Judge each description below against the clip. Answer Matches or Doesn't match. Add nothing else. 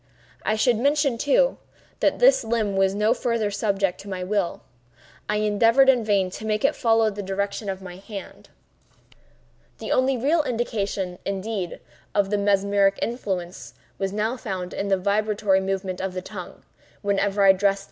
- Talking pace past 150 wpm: Matches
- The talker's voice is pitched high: Matches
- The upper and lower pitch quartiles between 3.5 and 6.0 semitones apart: Doesn't match